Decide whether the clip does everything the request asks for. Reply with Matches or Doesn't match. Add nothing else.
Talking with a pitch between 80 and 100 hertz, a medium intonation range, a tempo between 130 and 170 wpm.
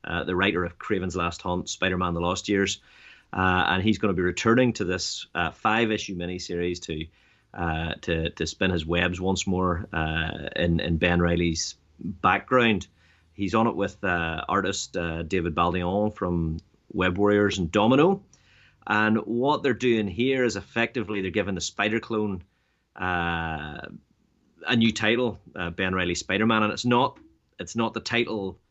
Matches